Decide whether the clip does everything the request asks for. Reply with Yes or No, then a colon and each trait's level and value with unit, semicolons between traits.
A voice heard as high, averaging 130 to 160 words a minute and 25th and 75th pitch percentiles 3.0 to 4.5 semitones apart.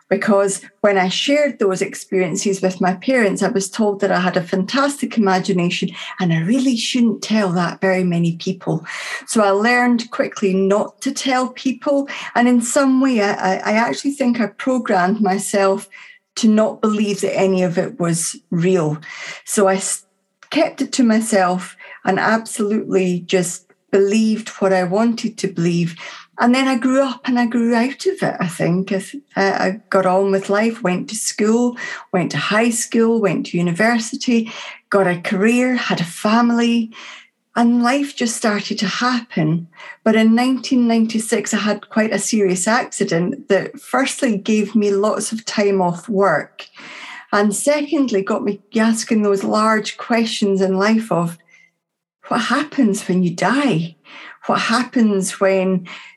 Yes: high, 210 Hz; average, 155 wpm; average, 4.0 semitones